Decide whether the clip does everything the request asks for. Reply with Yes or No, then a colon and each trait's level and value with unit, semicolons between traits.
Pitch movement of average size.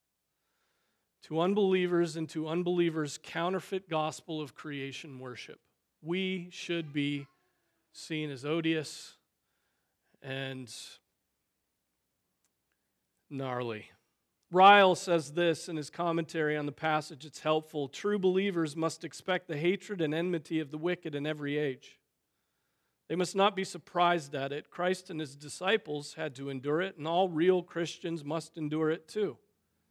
Yes: average, 3.0 semitones